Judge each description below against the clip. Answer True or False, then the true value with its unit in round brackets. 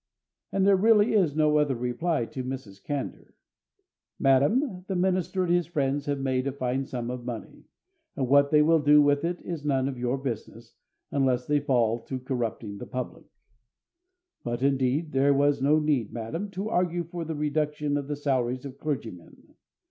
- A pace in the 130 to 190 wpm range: True (180 wpm)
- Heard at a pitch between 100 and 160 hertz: True (140 Hz)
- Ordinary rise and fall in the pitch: True (3.7 semitones)